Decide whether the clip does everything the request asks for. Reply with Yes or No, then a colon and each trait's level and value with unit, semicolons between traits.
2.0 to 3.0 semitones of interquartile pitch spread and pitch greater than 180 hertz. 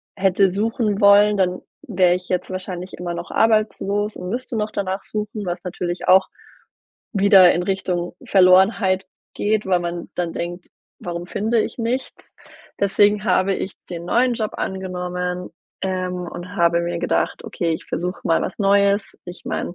Yes: narrow, 2.5 semitones; high, 190 Hz